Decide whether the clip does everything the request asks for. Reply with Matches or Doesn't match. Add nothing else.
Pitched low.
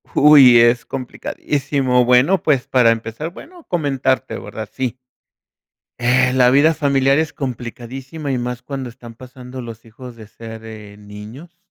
Matches